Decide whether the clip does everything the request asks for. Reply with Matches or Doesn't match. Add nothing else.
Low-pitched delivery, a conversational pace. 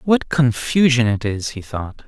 Matches